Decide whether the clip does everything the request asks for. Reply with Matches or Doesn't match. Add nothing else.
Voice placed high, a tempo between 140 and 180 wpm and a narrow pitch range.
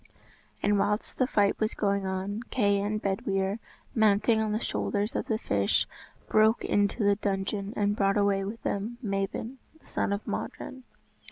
Matches